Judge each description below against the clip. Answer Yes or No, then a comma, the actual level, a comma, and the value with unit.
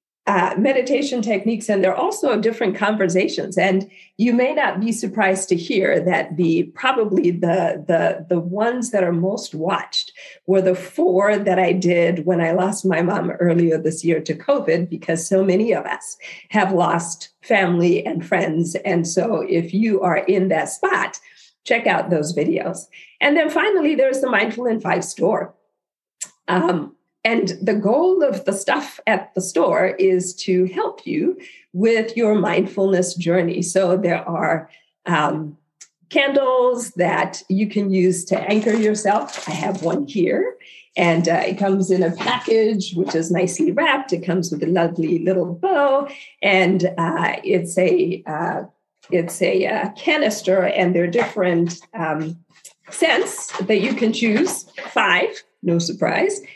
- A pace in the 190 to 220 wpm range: No, average, 155 wpm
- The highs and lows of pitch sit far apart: No, average, 4.3 semitones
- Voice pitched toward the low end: No, high, 190 Hz